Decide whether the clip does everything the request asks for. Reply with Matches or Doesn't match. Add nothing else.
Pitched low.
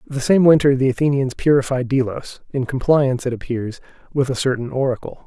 Matches